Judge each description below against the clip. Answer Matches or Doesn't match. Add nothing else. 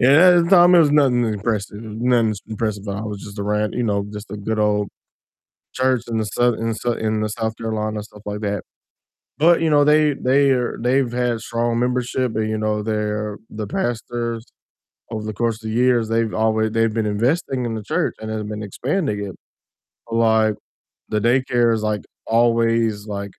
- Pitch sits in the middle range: Doesn't match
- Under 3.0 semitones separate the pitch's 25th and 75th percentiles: Matches